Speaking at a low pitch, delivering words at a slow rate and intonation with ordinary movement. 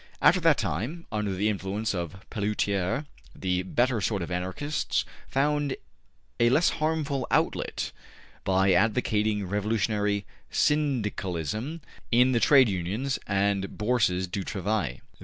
Yes: low, 105 Hz; slow, 120 wpm; average, 4.9 semitones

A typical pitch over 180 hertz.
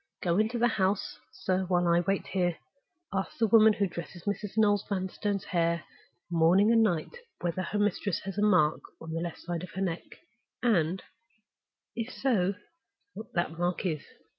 Yes: high, 190 Hz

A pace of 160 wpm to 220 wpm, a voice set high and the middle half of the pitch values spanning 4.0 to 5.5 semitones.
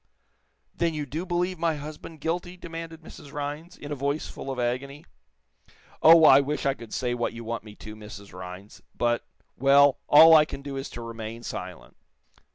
No: average, 185 wpm; medium, 140 Hz; average, 5.2 semitones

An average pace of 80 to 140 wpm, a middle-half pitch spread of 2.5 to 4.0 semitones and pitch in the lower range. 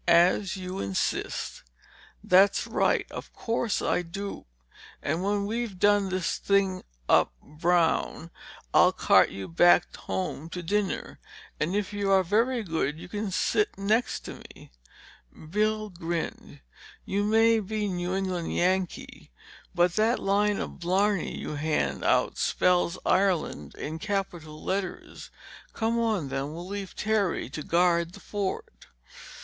No: slow, 135 wpm; average, 3.2 semitones; high, 190 Hz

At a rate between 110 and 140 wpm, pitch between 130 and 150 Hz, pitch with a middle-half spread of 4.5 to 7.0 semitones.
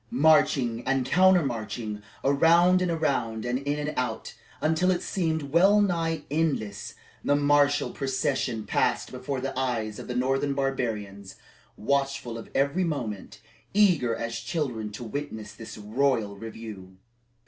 Yes: slow, 135 wpm; low, 135 Hz; average, 5.1 semitones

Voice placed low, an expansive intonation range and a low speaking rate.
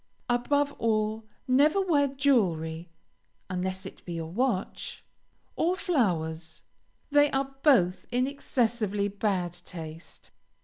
No: high, 220 Hz; wide, 7.5 semitones; slow, 105 wpm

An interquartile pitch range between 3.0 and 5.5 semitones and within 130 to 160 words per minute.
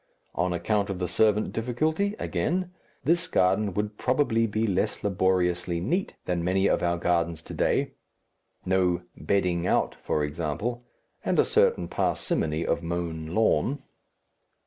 Yes: average, 4.5 semitones; average, 140 wpm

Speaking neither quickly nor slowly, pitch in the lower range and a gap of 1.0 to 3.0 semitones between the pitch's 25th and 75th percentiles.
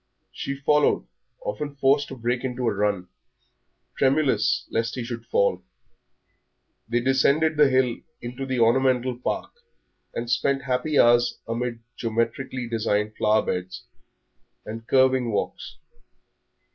No: slow, 120 wpm; low, 125 Hz; narrow, 2.6 semitones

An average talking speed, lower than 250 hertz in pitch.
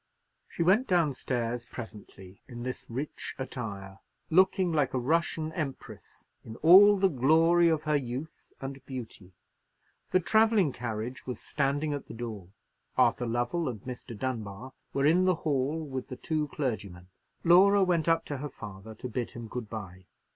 Yes: average, 160 wpm; low, 135 Hz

